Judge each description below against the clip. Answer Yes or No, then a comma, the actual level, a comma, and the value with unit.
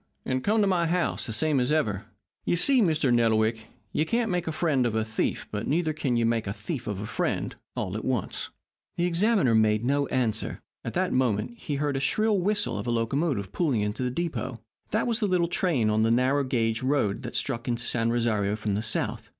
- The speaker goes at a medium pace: No, fast, 225 wpm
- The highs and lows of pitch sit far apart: Yes, wide, 6.7 semitones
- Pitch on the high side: No, low, 130 Hz